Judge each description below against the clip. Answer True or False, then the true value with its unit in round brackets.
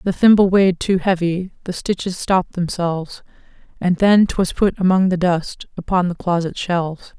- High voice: False (180 Hz)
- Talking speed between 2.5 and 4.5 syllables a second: False (5.1 syllables/s)